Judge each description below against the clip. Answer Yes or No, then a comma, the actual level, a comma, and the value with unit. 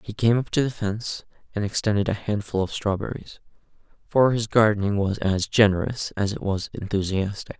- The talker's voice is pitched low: Yes, low, 105 Hz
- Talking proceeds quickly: No, average, 175 wpm